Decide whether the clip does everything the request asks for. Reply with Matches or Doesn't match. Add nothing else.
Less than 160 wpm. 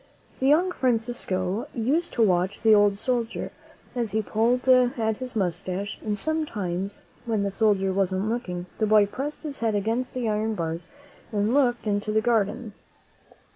Doesn't match